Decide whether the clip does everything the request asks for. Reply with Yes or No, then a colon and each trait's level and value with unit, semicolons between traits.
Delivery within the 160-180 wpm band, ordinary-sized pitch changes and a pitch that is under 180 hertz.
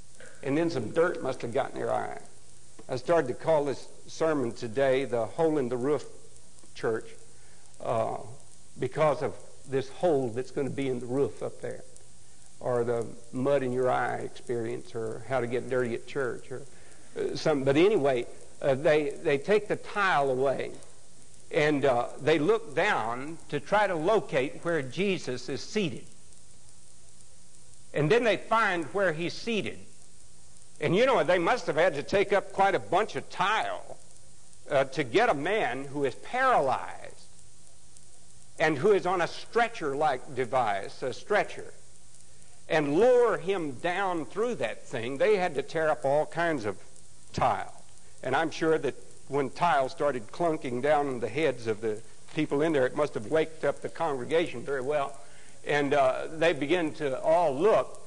No: average, 165 wpm; wide, 7.2 semitones; medium, 140 Hz